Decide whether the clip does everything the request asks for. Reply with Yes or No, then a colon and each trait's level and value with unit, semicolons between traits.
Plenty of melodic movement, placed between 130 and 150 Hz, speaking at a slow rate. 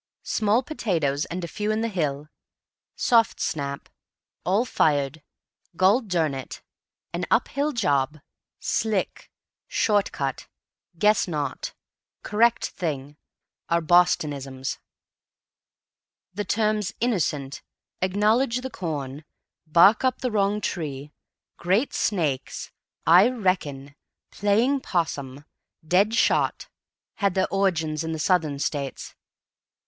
No: wide, 6.4 semitones; medium, 180 Hz; slow, 105 wpm